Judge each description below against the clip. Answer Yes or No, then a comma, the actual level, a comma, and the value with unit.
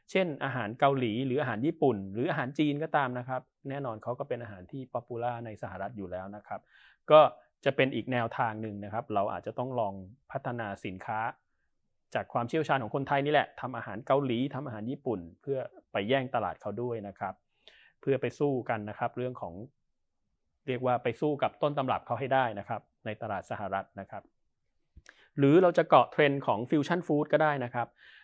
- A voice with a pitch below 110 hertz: No, low, 125 Hz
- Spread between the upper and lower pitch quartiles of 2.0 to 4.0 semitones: No, average, 4.5 semitones